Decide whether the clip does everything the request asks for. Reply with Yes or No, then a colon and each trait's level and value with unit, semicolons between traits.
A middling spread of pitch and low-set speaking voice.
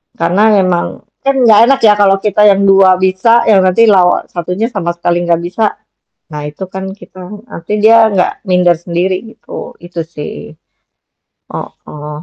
No: average, 3.3 semitones; high, 190 Hz